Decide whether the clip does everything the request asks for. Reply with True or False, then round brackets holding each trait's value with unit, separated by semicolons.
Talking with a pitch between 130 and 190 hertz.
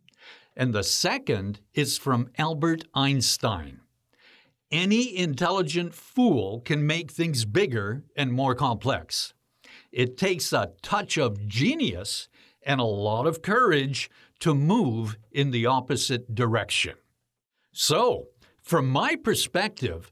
True (135 Hz)